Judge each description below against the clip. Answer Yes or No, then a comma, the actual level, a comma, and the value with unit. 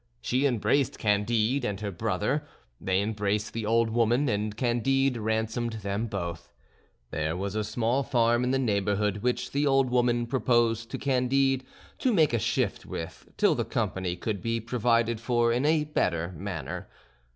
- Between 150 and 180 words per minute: Yes, average, 160 wpm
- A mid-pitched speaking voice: No, low, 115 Hz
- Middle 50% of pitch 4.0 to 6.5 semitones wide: No, average, 3.4 semitones